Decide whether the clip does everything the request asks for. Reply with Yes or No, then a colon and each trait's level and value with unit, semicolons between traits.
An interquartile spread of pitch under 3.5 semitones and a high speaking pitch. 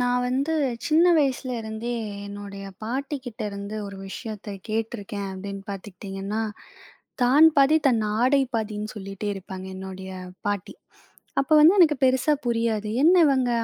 No: average, 4.7 semitones; high, 220 Hz